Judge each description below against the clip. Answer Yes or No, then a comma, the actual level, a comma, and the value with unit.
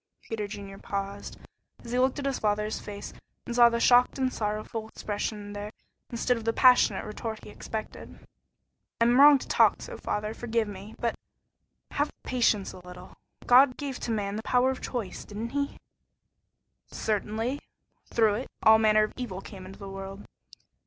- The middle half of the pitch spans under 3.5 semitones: Yes, average, 3.1 semitones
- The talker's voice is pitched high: Yes, high, 220 Hz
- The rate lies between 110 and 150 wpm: No, average, 175 wpm